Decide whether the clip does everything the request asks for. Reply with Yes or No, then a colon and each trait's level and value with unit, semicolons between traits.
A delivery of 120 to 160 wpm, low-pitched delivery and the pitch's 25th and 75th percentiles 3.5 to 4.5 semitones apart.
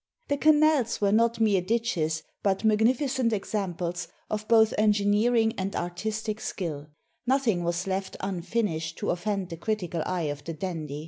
No: average, 155 wpm; high, 200 Hz; average, 4.2 semitones